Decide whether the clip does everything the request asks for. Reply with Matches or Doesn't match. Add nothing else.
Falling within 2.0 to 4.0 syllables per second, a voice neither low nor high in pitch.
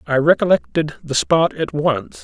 Doesn't match